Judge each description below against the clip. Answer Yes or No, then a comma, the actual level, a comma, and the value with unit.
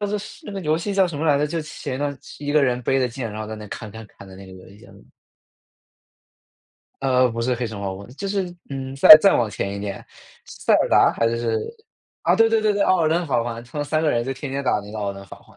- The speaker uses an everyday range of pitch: No, wide, 6.2 semitones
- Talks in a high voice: No, low, 130 Hz